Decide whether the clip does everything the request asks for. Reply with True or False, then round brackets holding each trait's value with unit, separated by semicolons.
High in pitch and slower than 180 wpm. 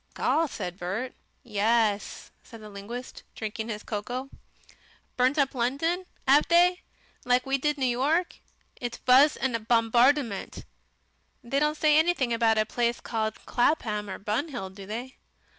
True (245 Hz; 145 wpm)